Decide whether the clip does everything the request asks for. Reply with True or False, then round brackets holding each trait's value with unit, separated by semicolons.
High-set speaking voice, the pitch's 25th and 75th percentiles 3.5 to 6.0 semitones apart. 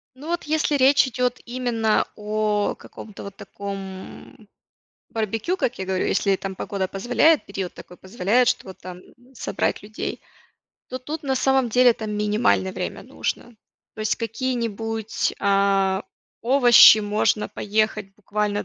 True (215 Hz; 3.8 semitones)